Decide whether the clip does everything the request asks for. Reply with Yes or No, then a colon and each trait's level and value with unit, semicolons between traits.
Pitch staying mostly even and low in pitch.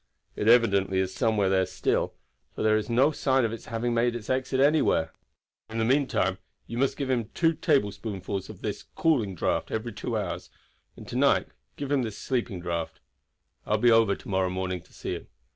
No: average, 5.0 semitones; low, 115 Hz